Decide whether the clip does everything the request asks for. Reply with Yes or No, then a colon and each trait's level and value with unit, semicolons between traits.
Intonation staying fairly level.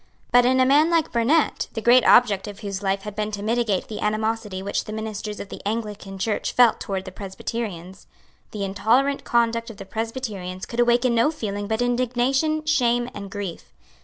No: average, 3.3 semitones